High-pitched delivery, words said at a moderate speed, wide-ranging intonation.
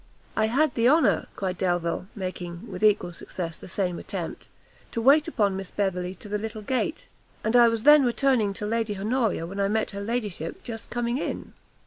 No: high, 215 Hz; average, 190 wpm; average, 4.1 semitones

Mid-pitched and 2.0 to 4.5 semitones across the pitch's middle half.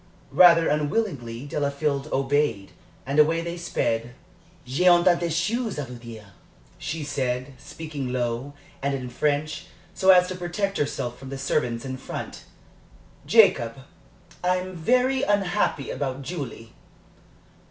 No: medium, 145 Hz; average, 5.1 semitones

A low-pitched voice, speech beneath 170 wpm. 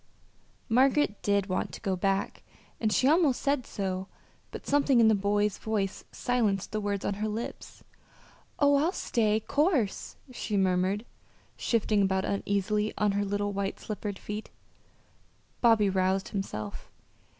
No: high, 205 Hz; average, 140 wpm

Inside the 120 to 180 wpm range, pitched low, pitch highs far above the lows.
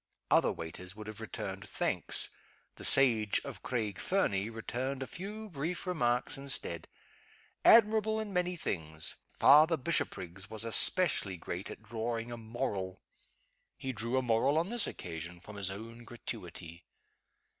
Yes: average, 140 wpm; low, 115 Hz; wide, 7.6 semitones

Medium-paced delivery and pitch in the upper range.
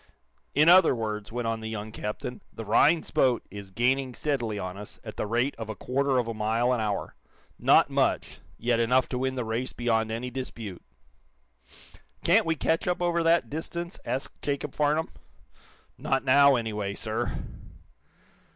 No: average, 170 wpm; low, 120 Hz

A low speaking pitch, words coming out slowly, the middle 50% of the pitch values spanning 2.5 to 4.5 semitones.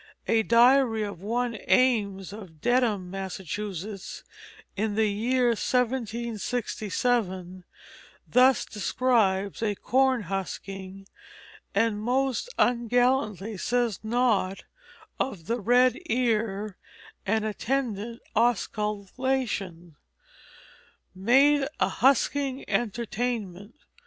No: high, 220 Hz; slow, 80 wpm; average, 3.9 semitones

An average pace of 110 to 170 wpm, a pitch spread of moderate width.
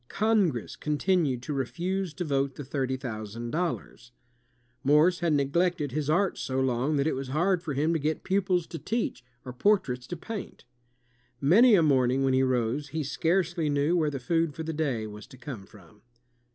No: average, 185 wpm; average, 5.0 semitones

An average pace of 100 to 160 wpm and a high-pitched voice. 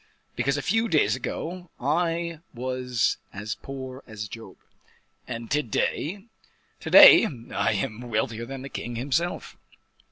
No: slow, 135 wpm; low, 130 Hz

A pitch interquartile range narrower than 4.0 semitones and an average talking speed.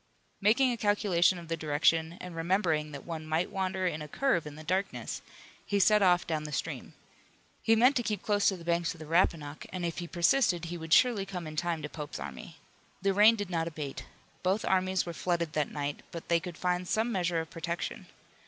No: average, 3.2 semitones; fast, 220 wpm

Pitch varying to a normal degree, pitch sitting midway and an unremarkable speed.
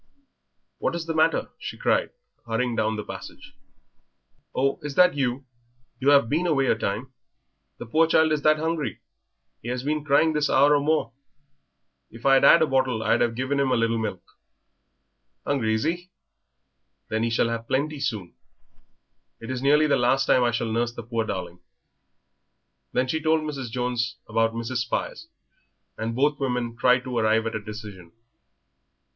No: average, 4.2 semitones; low, 125 Hz; average, 175 wpm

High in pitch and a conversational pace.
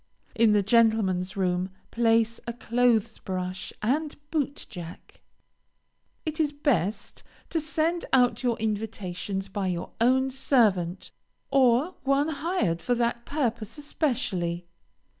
No: high, 230 Hz; slow, 120 wpm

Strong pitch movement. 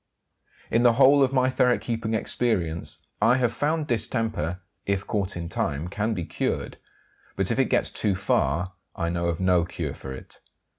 Yes: wide, 6.0 semitones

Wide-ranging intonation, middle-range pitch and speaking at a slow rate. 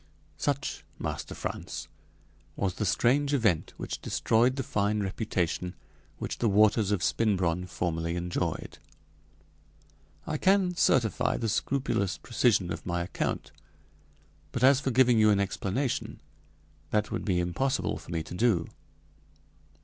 No: wide, 5.9 semitones; low, 105 Hz; slow, 130 wpm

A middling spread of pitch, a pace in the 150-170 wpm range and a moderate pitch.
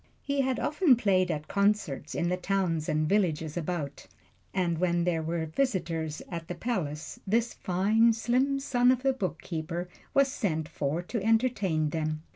No: wide, 6.2 semitones; average, 160 wpm; medium, 180 Hz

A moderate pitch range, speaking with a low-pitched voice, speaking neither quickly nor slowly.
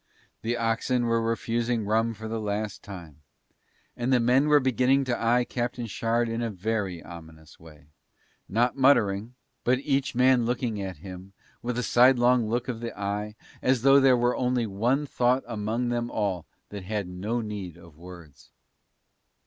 Yes: average, 3.5 semitones; low, 115 Hz; average, 165 wpm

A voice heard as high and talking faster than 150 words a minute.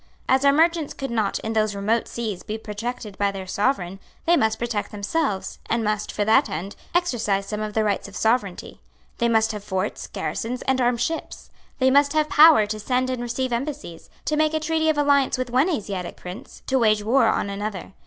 Yes: high, 230 Hz; fast, 205 wpm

